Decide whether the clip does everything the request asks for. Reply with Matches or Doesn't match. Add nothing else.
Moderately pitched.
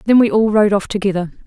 Doesn't match